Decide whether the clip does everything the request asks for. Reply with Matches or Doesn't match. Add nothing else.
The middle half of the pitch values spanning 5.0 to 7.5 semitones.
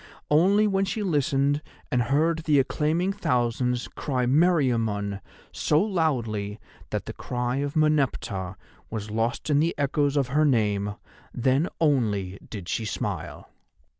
Matches